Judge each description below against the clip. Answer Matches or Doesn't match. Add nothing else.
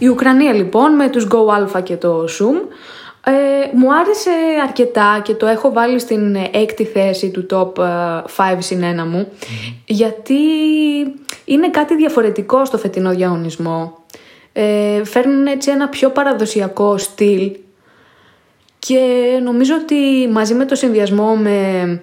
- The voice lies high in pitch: Matches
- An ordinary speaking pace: Matches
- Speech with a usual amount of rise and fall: Doesn't match